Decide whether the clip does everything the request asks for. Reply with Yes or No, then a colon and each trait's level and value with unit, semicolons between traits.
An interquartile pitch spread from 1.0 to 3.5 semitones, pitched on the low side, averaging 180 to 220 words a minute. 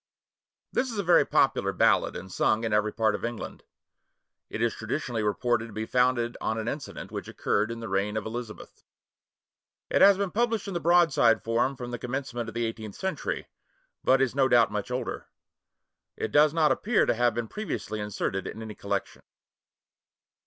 No: average, 4.1 semitones; low, 120 Hz; average, 185 wpm